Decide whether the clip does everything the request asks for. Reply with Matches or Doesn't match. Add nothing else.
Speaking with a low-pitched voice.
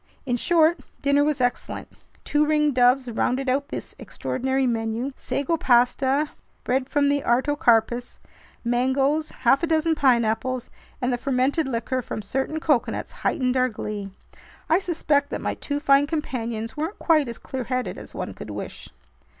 Doesn't match